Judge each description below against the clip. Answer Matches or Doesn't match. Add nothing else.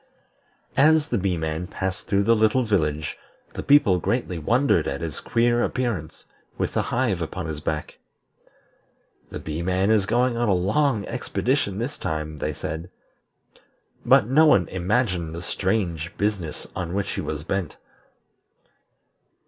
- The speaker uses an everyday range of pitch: Doesn't match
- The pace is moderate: Matches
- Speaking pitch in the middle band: Doesn't match